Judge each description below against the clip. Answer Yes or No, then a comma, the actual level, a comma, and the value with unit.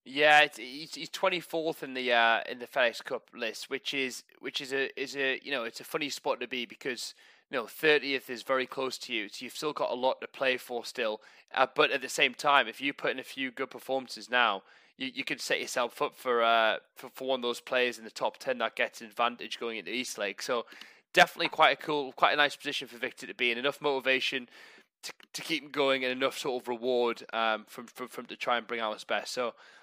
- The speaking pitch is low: Yes, low, 130 Hz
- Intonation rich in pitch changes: No, average, 2.7 semitones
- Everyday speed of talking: No, fast, 255 wpm